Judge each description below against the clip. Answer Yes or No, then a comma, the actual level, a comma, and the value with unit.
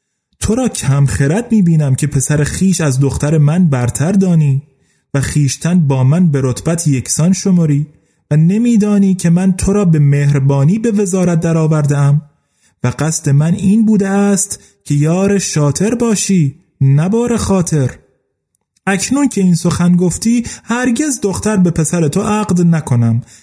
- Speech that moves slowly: No, average, 150 wpm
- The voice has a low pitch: No, medium, 165 Hz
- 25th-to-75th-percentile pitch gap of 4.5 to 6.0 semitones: Yes, average, 5.3 semitones